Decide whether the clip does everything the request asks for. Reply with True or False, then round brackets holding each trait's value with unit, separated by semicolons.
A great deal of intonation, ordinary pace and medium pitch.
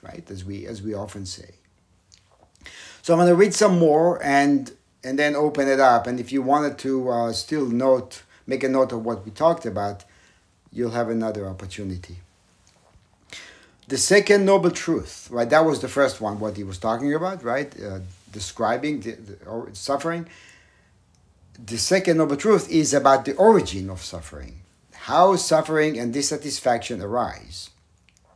False (7.2 semitones; 160 wpm; 120 Hz)